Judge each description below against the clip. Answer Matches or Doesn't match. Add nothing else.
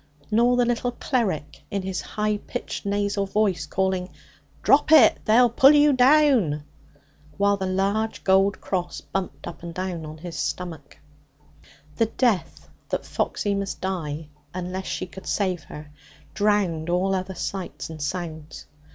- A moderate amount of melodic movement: Matches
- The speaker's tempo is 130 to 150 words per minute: Matches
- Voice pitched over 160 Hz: Matches